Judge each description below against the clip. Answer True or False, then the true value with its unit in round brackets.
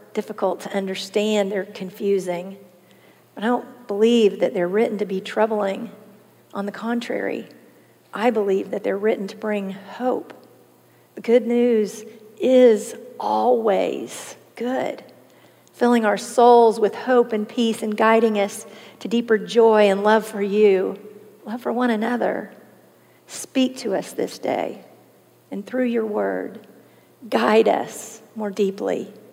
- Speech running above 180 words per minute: False (135 wpm)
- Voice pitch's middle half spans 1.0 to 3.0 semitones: True (2.6 semitones)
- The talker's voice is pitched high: True (215 Hz)